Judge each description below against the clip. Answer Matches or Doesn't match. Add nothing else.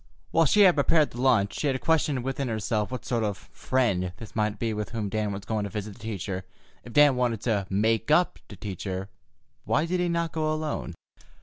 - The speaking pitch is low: Matches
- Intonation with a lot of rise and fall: Matches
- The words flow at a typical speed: Doesn't match